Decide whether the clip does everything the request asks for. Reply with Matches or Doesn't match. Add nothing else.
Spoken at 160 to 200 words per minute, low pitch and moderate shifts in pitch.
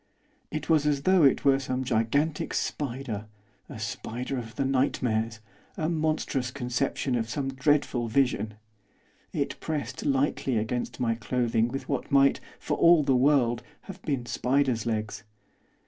Doesn't match